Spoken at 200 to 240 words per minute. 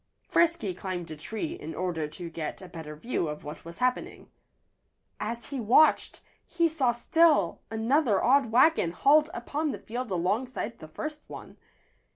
No: average, 160 wpm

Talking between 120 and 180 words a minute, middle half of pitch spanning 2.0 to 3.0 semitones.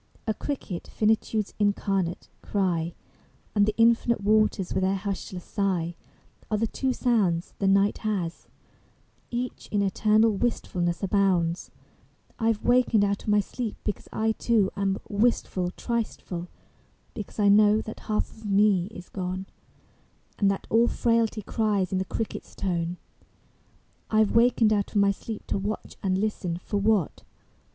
Yes: average, 150 wpm; narrow, 2.6 semitones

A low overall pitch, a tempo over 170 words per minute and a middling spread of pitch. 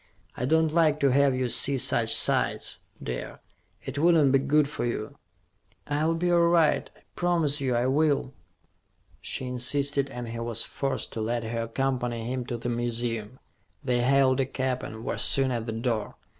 Yes: low, 130 Hz; average, 180 wpm; average, 3.1 semitones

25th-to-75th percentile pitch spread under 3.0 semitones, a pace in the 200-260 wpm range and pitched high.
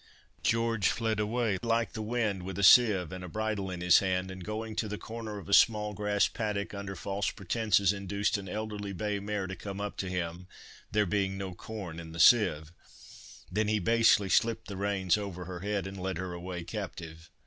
No: narrow, 2.6 semitones; fast, 205 wpm; low, 100 Hz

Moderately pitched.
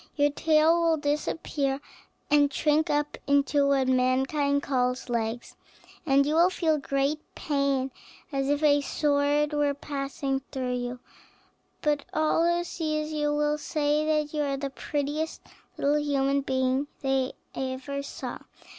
No: very high, 285 Hz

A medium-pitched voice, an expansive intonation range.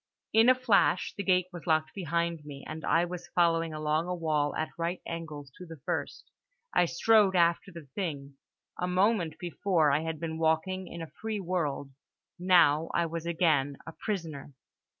No: medium, 170 Hz; narrow, 2.5 semitones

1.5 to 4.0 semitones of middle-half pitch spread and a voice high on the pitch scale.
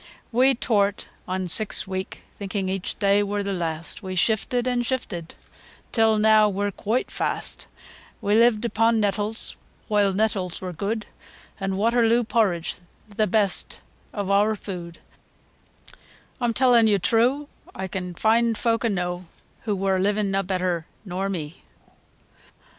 Yes: average, 3.0 semitones; high, 205 Hz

